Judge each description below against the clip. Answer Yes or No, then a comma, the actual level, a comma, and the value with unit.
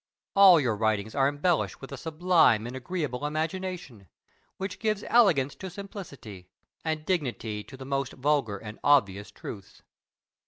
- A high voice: No, medium, 140 Hz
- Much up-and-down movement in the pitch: Yes, wide, 7.9 semitones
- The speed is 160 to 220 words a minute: No, average, 145 wpm